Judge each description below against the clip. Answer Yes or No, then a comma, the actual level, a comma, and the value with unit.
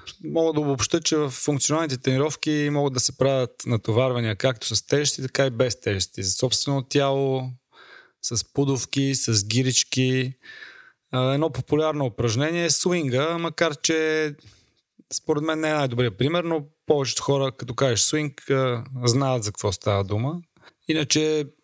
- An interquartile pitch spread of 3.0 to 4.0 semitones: Yes, average, 3.3 semitones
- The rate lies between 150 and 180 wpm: No, average, 140 wpm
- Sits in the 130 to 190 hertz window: Yes, low, 135 Hz